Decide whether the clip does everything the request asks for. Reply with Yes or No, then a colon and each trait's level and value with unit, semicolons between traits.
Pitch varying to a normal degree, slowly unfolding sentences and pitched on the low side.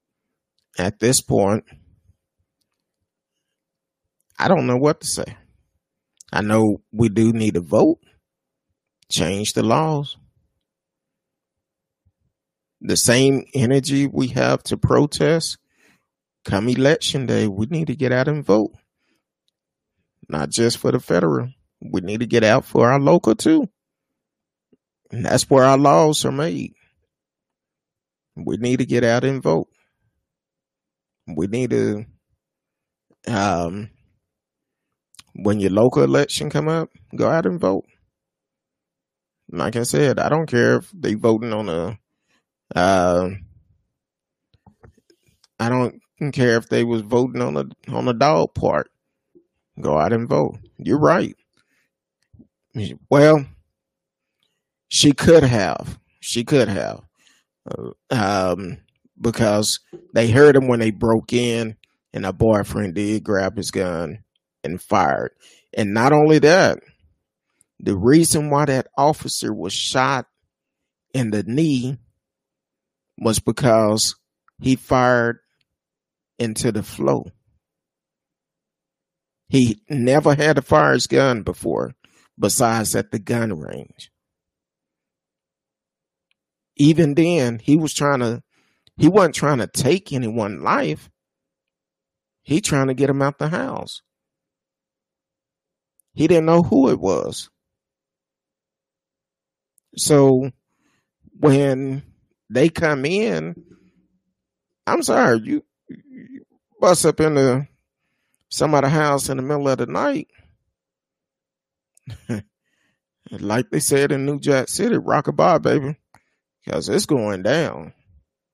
Yes: average, 4.8 semitones; slow, 115 wpm; low, 125 Hz